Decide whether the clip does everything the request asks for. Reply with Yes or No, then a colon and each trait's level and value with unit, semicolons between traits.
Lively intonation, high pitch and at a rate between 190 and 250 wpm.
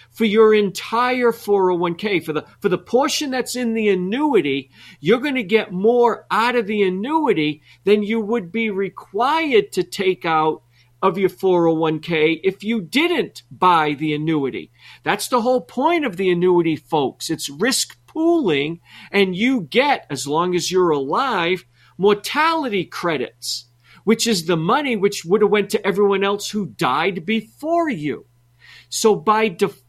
No: wide, 6.0 semitones; high, 200 Hz; average, 155 wpm